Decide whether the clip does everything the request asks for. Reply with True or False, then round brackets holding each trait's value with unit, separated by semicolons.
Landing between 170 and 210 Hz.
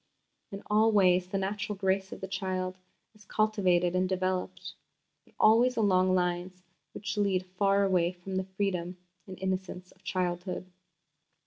True (190 Hz)